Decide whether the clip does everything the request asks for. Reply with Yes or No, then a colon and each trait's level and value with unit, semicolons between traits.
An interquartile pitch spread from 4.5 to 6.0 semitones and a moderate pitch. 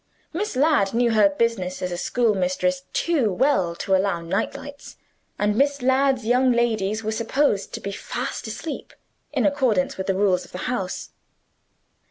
No: wide, 5.5 semitones; high, 220 Hz